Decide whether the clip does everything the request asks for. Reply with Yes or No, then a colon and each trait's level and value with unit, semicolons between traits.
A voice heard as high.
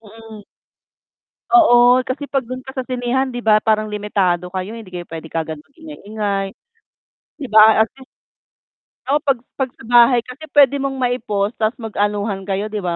Yes: high, 220 Hz